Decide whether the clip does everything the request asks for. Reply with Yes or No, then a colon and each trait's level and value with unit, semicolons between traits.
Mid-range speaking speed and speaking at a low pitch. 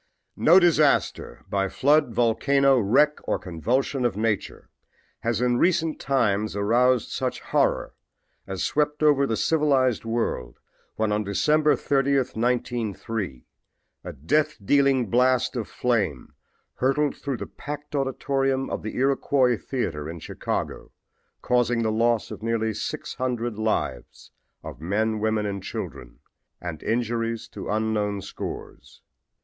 No: slow, 125 wpm; low, 120 Hz